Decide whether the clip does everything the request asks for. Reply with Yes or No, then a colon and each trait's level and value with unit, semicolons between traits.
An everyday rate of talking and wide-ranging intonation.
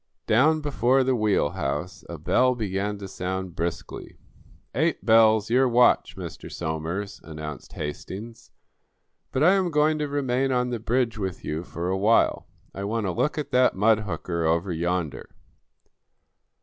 Yes: average, 150 wpm; wide, 6.2 semitones